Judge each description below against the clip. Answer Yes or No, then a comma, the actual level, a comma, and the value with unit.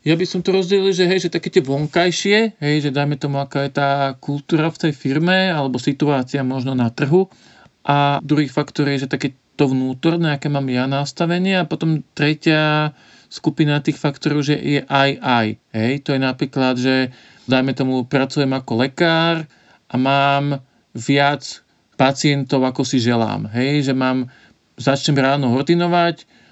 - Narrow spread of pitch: No, average, 3.0 semitones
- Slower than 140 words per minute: No, fast, 165 wpm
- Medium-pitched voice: Yes, medium, 145 Hz